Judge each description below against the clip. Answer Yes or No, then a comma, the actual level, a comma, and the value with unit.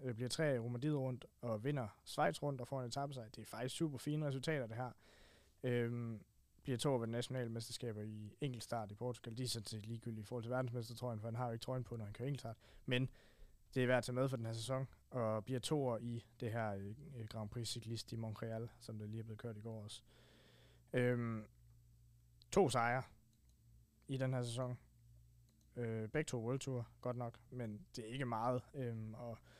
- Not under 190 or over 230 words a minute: Yes, average, 210 wpm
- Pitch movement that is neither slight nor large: No, narrow, 2.2 semitones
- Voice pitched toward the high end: No, low, 120 Hz